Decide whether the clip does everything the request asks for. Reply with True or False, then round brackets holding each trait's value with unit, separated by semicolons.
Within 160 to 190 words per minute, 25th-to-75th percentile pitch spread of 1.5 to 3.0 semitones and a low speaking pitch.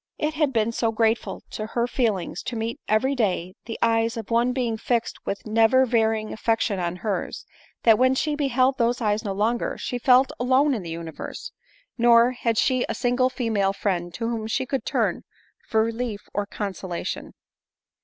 False (185 wpm; 2.7 semitones; 230 Hz)